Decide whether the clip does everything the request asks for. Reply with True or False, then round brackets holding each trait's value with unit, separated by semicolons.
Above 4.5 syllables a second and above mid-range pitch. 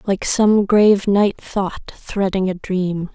False (3.5 syllables/s; 195 Hz)